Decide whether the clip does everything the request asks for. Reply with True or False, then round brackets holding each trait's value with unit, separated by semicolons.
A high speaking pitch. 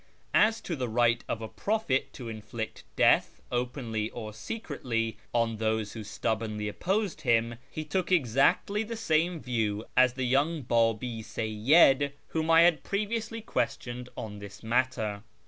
False (125 Hz)